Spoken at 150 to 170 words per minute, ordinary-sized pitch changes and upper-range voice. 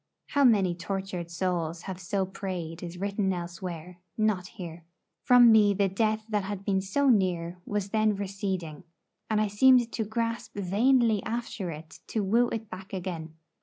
Yes: average, 165 wpm; average, 3.3 semitones; high, 195 Hz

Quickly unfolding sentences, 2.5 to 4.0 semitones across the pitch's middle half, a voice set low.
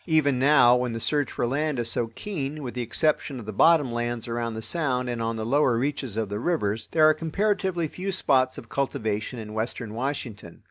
No: fast, 215 wpm; average, 4.7 semitones; low, 125 Hz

